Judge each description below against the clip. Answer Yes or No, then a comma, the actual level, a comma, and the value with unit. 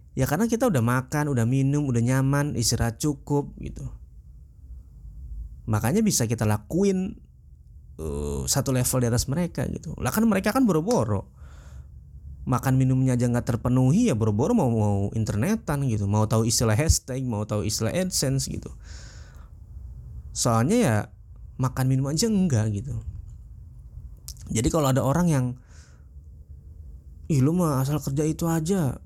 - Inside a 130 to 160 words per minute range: Yes, fast, 140 wpm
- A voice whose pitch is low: Yes, low, 115 Hz